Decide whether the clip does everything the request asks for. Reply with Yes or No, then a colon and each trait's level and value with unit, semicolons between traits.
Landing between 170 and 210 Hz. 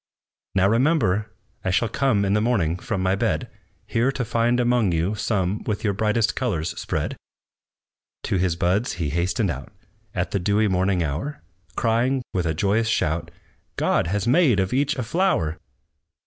No: low, 105 Hz